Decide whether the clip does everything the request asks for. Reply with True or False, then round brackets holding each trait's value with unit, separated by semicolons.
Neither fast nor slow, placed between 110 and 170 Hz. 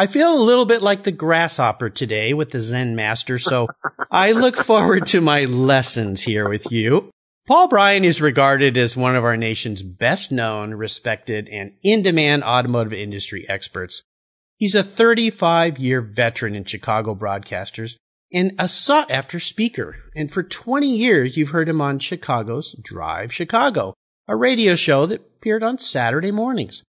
True (160 wpm; 140 Hz)